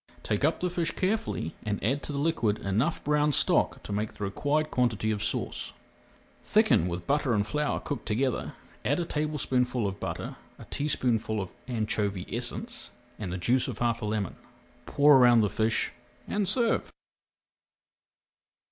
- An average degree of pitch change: No, wide, 5.9 semitones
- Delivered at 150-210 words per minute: Yes, average, 160 wpm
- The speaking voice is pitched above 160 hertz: No, low, 120 Hz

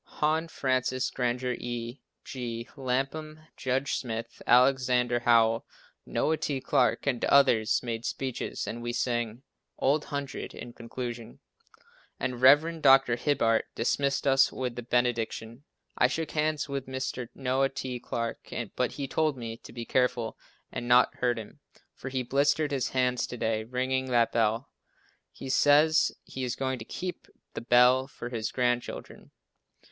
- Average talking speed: Yes, average, 150 wpm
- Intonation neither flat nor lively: No, narrow, 2.3 semitones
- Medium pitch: No, low, 125 Hz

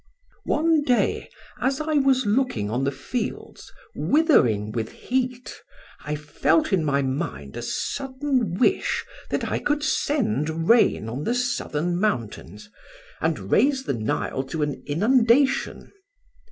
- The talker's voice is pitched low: No, high, 210 Hz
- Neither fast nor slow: No, slow, 130 wpm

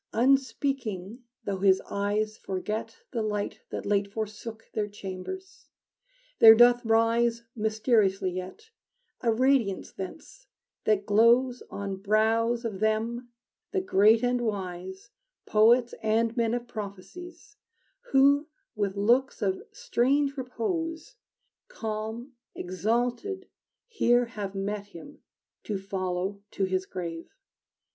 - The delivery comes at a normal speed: No, slow, 110 wpm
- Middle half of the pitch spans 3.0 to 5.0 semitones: Yes, average, 3.4 semitones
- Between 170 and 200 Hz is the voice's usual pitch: No, high, 220 Hz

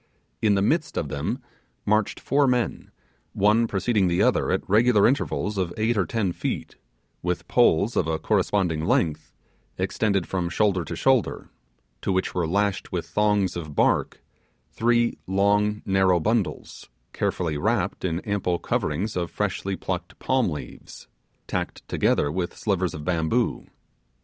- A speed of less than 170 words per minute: Yes, average, 145 wpm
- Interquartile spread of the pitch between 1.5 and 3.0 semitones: No, average, 3.7 semitones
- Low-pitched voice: Yes, very low, 95 Hz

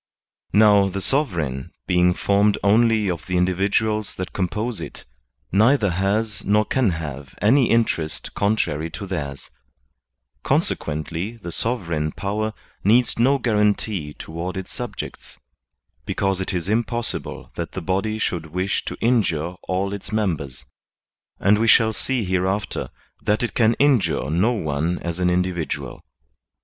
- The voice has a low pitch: Yes, low, 100 Hz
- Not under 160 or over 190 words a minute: No, slow, 135 wpm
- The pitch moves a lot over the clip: No, average, 3.9 semitones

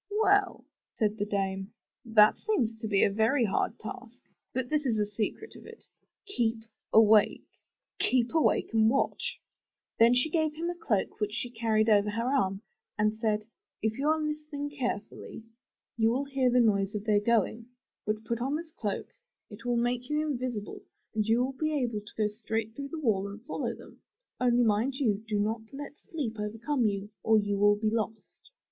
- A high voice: Yes, high, 225 Hz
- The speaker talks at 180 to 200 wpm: Yes, average, 195 wpm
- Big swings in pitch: No, average, 4.3 semitones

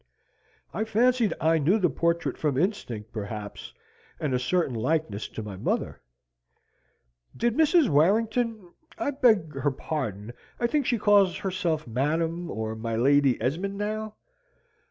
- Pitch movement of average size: No, wide, 8.8 semitones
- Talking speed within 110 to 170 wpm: Yes, slow, 135 wpm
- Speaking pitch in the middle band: Yes, medium, 165 Hz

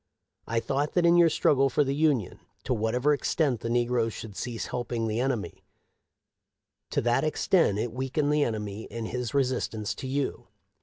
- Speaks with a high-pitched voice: No, low, 125 Hz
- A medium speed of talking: Yes, average, 185 wpm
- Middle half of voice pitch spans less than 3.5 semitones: No, average, 4.0 semitones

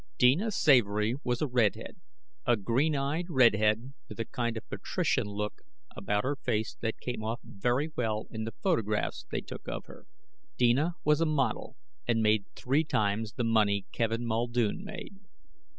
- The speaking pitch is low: Yes, low, 120 Hz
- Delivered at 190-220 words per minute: No, average, 165 wpm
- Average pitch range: Yes, average, 4.1 semitones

